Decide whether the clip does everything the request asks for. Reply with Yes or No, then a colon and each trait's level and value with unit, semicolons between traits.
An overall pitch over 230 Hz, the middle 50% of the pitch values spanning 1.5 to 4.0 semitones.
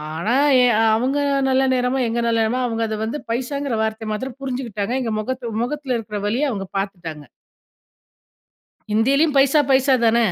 Yes: high, 240 Hz; average, 3.4 semitones